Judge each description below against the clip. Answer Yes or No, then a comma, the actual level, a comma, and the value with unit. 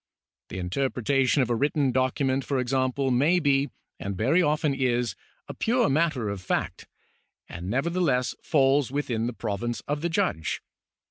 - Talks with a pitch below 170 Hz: Yes, low, 135 Hz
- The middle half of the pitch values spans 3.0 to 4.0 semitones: Yes, average, 3.4 semitones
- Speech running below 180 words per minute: Yes, average, 150 wpm